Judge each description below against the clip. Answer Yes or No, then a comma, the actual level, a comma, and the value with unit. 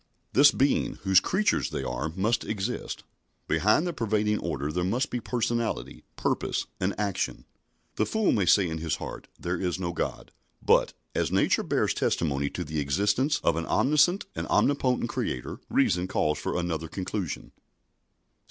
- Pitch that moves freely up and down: Yes, wide, 6.3 semitones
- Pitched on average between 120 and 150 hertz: No, very low, 95 Hz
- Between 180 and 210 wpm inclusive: No, average, 160 wpm